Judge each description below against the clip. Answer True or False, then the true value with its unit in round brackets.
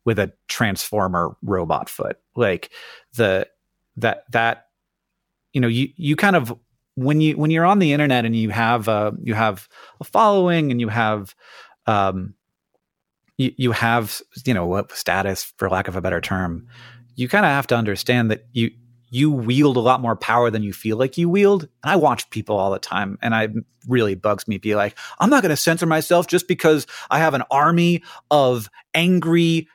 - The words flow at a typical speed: True (190 wpm)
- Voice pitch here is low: True (120 Hz)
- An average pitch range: False (5.9 semitones)